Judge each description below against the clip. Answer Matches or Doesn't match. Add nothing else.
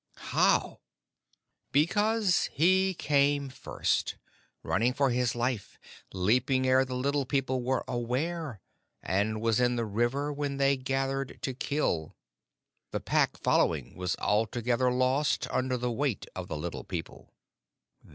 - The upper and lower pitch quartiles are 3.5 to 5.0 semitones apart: Doesn't match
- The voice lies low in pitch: Matches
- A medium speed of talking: Doesn't match